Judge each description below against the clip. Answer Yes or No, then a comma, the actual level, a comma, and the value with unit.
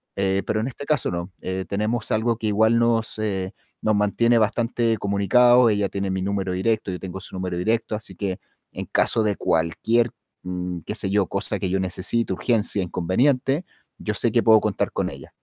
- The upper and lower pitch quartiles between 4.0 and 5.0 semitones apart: No, average, 3.3 semitones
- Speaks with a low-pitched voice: Yes, low, 105 Hz